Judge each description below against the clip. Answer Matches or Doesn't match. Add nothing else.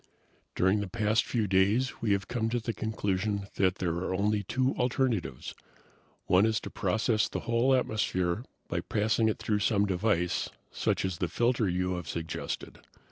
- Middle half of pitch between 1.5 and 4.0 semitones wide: Matches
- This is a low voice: Matches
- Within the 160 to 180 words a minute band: Matches